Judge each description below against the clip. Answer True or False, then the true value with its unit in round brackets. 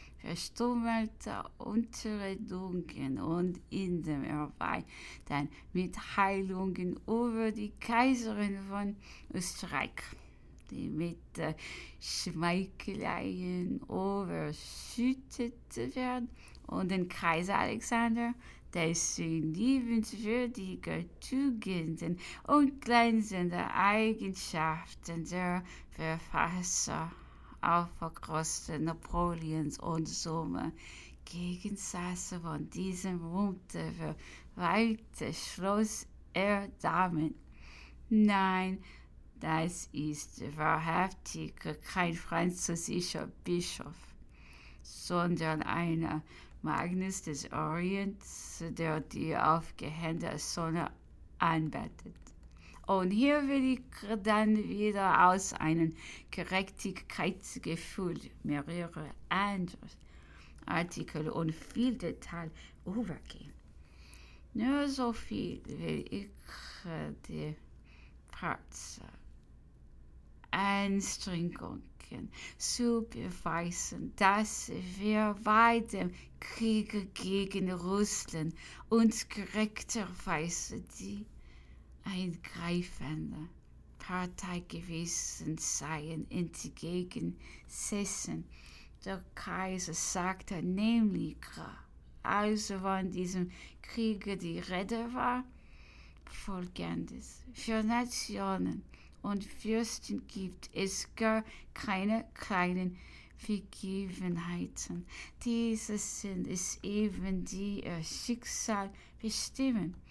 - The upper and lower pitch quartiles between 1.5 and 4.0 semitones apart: False (4.7 semitones)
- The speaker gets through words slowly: True (75 wpm)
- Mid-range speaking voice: True (180 Hz)